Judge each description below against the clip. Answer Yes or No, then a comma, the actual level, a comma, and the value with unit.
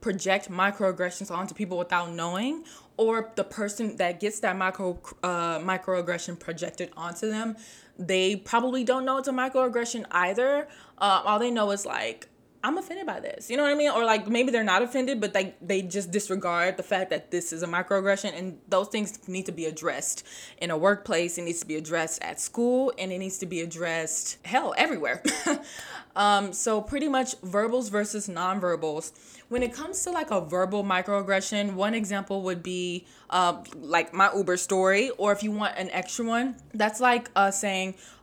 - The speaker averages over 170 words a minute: Yes, average, 190 wpm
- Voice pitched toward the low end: No, high, 195 Hz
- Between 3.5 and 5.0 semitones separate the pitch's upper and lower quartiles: Yes, average, 3.9 semitones